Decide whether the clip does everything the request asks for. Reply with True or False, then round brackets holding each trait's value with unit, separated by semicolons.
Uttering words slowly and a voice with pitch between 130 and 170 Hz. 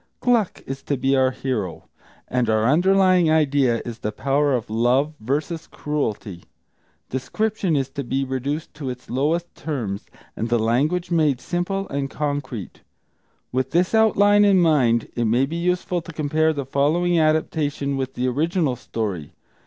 False (155 wpm; 140 Hz)